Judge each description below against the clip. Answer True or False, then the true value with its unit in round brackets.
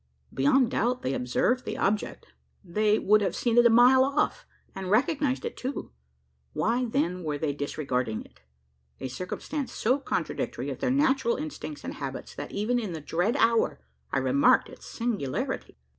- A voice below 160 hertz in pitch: False (225 Hz)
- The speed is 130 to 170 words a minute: True (165 wpm)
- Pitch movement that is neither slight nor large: False (7.2 semitones)